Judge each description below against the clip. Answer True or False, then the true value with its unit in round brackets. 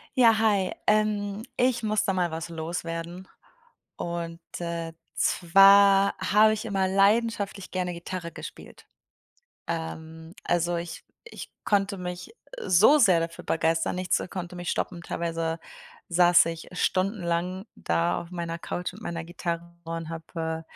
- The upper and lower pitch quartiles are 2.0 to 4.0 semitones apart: True (2.9 semitones)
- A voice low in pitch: False (175 Hz)